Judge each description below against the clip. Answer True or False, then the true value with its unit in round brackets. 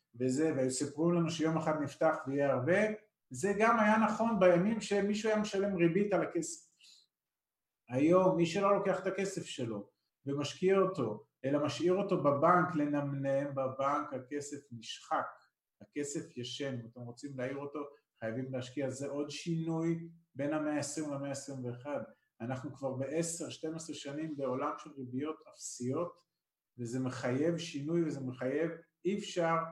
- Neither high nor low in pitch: True (150 Hz)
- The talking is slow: False (140 wpm)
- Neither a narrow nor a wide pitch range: True (4.0 semitones)